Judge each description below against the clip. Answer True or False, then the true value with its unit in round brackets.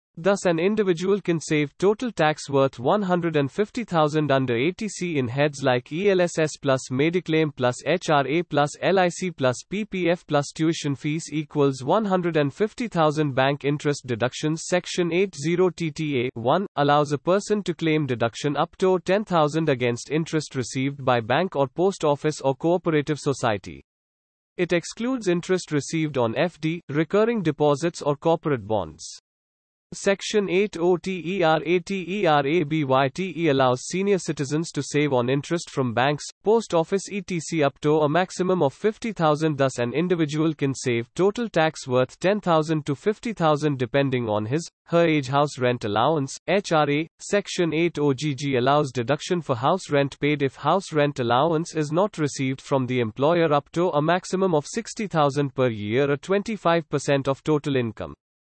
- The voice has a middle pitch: True (155 Hz)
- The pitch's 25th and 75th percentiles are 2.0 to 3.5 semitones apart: False (4.3 semitones)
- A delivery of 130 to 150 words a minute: True (140 wpm)